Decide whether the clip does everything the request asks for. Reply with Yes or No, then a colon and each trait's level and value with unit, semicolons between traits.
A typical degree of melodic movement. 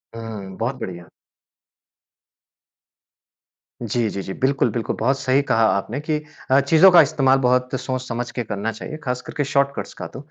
Yes: average, 3.6 semitones